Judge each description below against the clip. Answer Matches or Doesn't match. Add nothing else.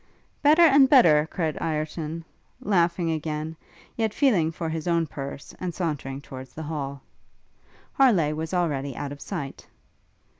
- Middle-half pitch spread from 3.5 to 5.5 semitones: Doesn't match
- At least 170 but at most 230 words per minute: Doesn't match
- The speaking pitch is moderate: Matches